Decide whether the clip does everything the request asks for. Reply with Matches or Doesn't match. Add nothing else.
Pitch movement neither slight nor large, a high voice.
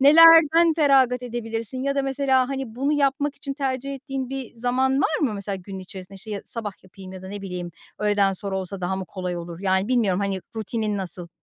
Doesn't match